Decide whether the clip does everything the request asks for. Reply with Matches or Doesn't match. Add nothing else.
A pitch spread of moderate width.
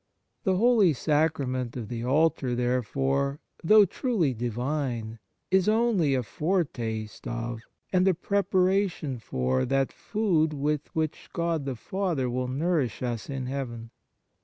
Doesn't match